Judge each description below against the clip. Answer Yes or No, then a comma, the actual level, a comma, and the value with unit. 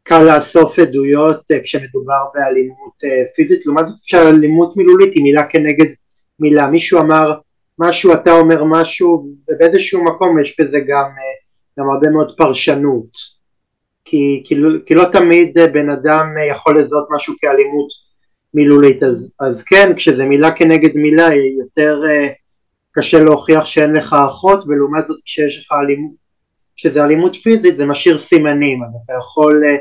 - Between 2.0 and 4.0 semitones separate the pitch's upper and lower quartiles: Yes, narrow, 2.5 semitones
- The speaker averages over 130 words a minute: Yes, average, 140 wpm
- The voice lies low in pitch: No, medium, 150 Hz